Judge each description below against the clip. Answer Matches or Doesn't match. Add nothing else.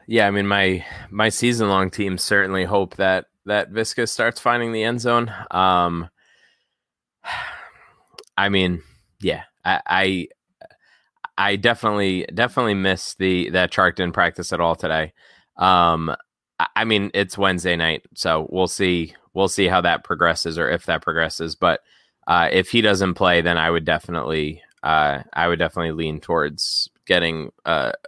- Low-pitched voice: Matches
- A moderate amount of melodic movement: Matches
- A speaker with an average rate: Matches